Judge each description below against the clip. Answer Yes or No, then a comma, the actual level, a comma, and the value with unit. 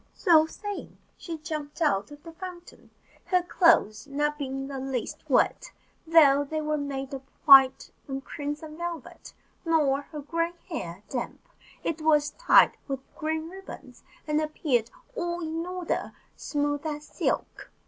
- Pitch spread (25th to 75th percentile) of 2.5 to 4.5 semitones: Yes, average, 3.0 semitones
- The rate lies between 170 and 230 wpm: No, average, 150 wpm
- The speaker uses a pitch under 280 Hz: No, very high, 300 Hz